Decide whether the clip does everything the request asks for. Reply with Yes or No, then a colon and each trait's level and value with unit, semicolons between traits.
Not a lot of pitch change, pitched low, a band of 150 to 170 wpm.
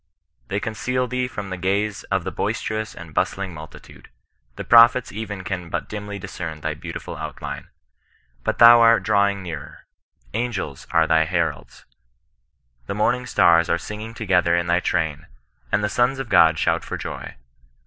No: average, 4.6 semitones; low, 100 Hz; average, 160 wpm